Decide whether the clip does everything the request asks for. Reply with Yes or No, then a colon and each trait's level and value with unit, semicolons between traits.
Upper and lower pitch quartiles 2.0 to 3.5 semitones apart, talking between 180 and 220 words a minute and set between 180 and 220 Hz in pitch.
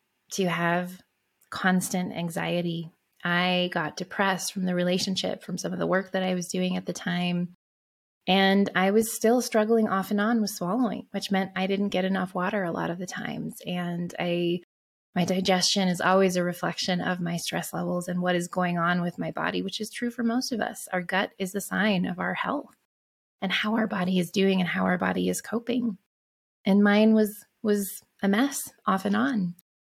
Yes: narrow, 2.6 semitones; average, 200 wpm; medium, 185 Hz